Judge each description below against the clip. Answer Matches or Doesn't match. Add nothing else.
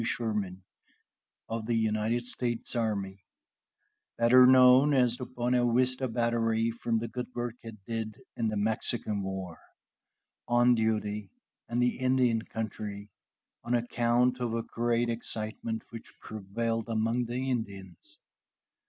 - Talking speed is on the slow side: Matches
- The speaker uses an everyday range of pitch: Doesn't match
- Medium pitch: Doesn't match